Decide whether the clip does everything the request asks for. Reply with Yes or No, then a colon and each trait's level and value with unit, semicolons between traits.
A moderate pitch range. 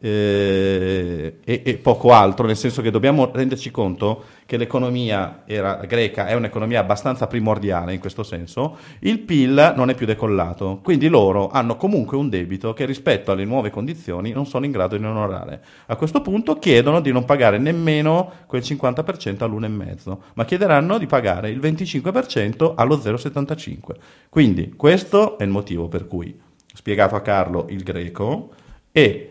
No: wide, 6.0 semitones